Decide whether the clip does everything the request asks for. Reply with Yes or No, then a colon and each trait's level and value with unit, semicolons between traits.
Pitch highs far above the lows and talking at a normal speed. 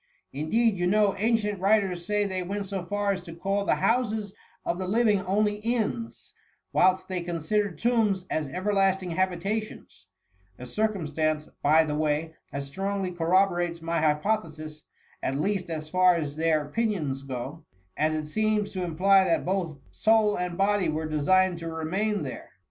No: average, 4.5 semitones; average, 165 wpm